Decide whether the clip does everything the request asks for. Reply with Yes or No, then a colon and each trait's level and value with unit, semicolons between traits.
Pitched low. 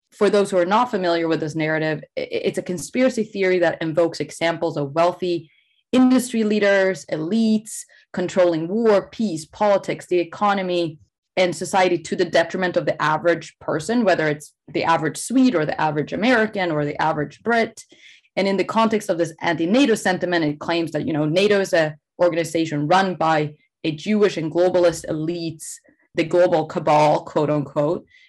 No: medium, 175 Hz